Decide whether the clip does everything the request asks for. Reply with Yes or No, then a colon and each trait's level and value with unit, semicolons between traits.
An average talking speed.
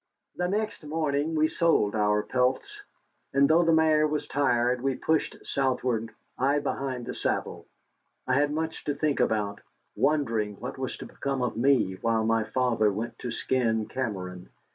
Yes: average, 165 wpm